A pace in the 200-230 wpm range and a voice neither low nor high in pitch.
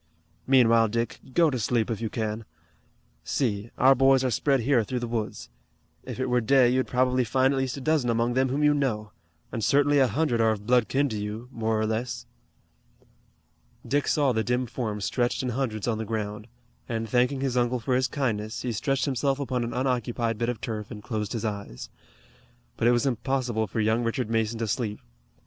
No: fast, 205 wpm; low, 120 Hz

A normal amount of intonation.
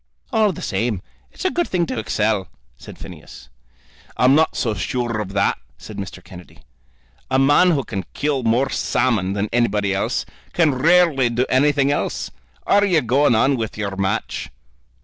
No: wide, 5.8 semitones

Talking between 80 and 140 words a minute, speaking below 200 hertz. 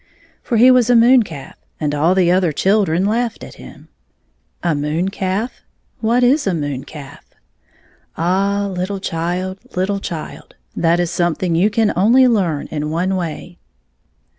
No: average, 155 wpm; medium, 185 Hz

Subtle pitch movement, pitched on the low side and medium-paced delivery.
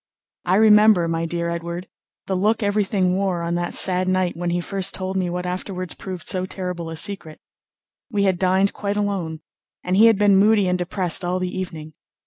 No: narrow, 2.2 semitones; medium, 185 Hz; average, 195 wpm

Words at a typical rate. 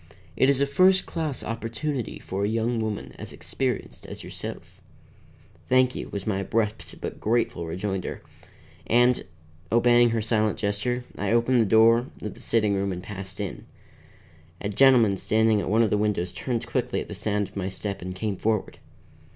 Yes: average, 175 wpm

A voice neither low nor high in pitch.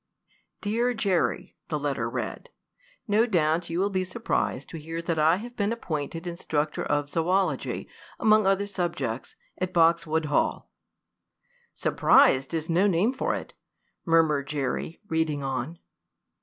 Yes: medium, 165 Hz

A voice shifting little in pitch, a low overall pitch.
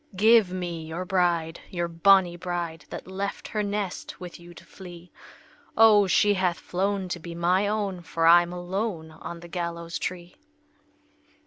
No: narrow, 2.2 semitones; medium, 180 Hz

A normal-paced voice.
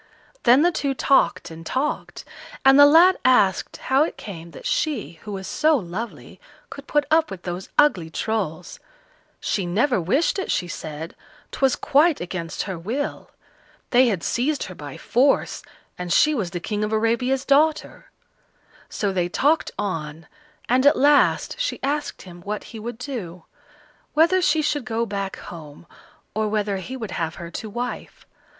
Yes: average, 165 wpm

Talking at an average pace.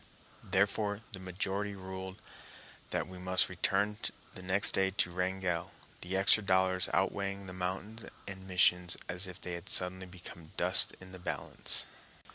Yes: average, 145 wpm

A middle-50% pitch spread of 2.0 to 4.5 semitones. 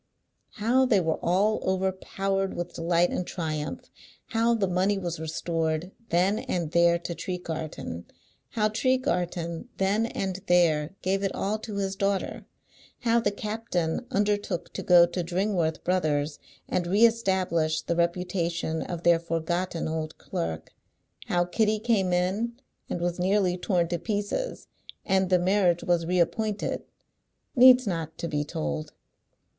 Yes: average, 3.2 semitones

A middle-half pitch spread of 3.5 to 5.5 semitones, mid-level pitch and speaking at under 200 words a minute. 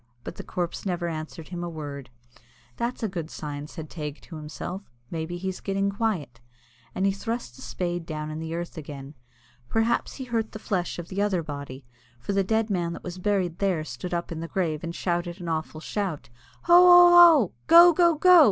No: average, 4.5 semitones; medium, 175 Hz; fast, 205 wpm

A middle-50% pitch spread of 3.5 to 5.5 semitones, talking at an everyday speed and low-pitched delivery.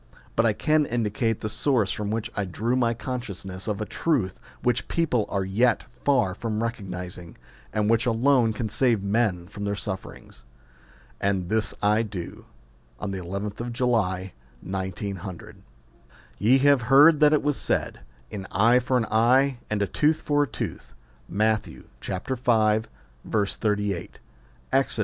Yes: average, 3.9 semitones; average, 150 wpm; low, 110 Hz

